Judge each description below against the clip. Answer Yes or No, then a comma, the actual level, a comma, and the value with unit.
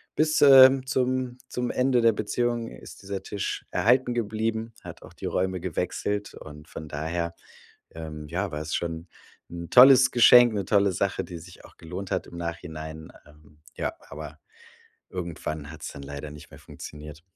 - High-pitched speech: No, very low, 90 Hz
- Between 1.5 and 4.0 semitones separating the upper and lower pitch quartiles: No, wide, 6.9 semitones